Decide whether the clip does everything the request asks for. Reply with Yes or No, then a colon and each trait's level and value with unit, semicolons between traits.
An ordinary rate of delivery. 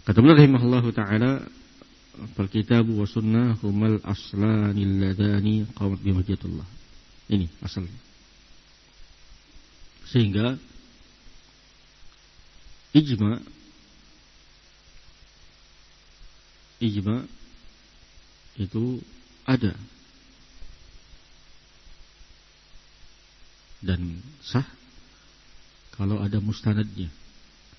No: slow, 55 wpm